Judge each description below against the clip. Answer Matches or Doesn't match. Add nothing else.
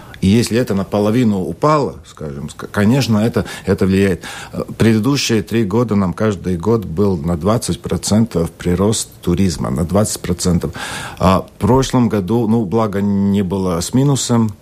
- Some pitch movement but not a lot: Matches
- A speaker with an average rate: Matches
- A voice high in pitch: Doesn't match